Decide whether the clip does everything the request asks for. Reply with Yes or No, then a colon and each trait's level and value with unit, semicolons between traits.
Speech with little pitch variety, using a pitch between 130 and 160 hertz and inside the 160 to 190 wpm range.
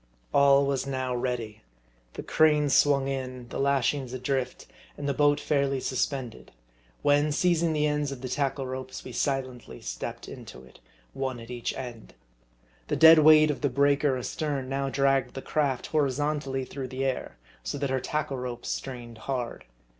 Yes: narrow, 2.2 semitones; low, 135 Hz; average, 170 wpm